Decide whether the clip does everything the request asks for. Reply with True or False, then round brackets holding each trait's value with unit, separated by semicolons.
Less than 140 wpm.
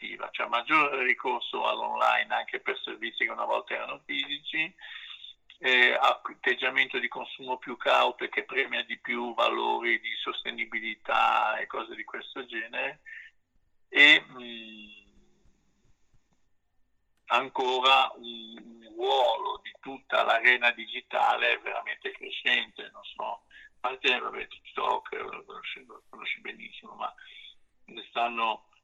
True (120 wpm)